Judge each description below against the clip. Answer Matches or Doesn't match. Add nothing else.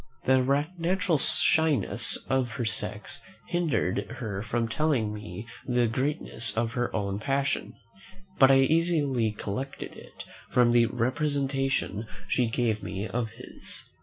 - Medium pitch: Doesn't match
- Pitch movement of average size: Matches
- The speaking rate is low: Matches